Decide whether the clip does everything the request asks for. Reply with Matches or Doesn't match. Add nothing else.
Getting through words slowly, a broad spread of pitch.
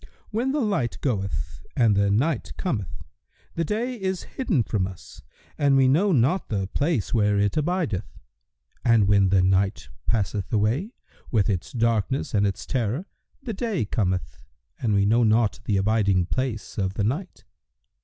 Doesn't match